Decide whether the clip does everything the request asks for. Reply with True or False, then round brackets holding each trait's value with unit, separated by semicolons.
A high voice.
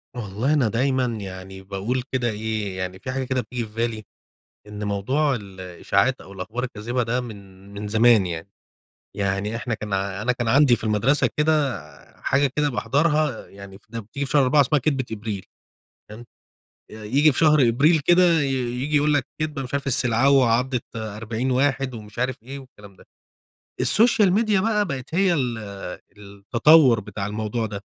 False (120 Hz)